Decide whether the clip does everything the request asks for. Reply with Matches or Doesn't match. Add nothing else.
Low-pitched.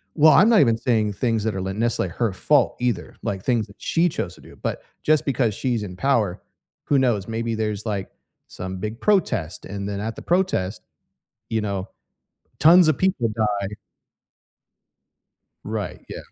Matches